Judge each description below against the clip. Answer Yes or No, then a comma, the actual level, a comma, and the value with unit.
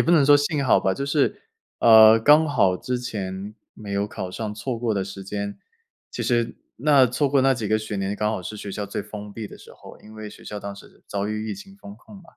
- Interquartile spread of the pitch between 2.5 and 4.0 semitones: No, average, 4.6 semitones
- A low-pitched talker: Yes, low, 110 Hz